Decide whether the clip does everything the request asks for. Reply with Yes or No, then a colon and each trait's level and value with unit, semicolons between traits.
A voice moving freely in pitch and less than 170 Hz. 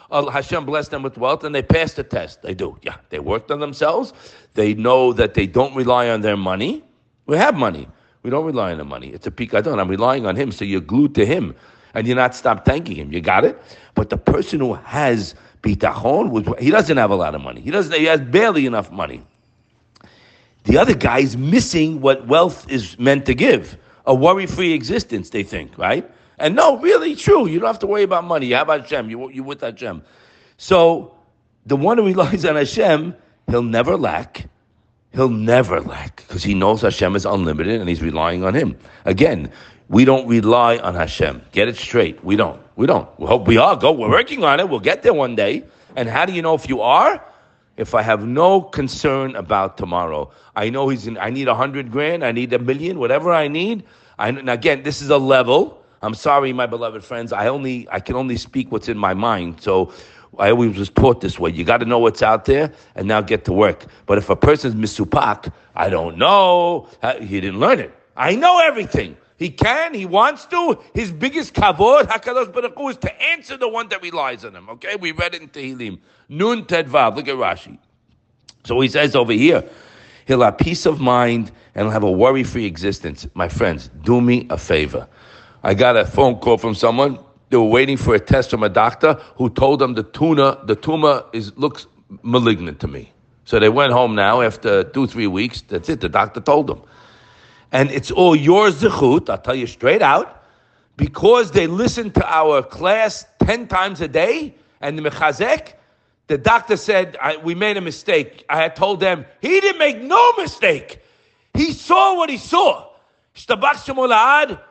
Yes: wide, 7.7 semitones; low, 135 Hz